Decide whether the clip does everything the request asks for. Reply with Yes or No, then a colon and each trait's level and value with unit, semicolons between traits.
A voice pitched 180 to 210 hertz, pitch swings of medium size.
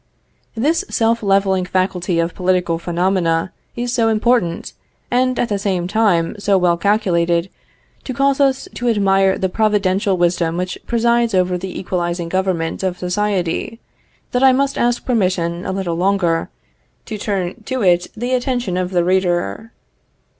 Yes: high, 190 Hz; average, 4.2 semitones